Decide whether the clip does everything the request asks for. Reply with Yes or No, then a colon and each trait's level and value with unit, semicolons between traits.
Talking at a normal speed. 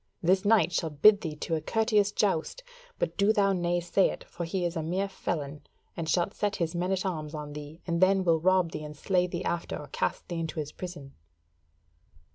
No: fast, 220 wpm